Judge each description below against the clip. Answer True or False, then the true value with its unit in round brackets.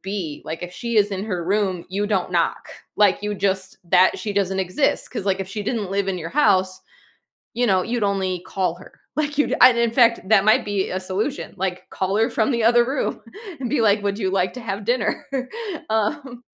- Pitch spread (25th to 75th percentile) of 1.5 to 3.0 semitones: False (3.6 semitones)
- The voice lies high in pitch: True (200 Hz)